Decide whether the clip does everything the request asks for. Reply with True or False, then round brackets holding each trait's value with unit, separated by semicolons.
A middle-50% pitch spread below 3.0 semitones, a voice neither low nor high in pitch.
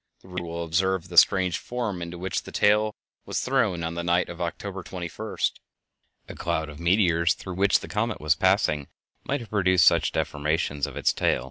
False (2.4 semitones; 90 Hz)